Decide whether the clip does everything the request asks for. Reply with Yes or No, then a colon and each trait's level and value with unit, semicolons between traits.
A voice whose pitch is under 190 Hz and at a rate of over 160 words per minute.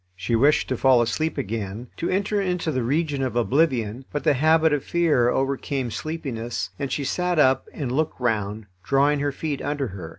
Yes: low, 135 Hz; average, 190 wpm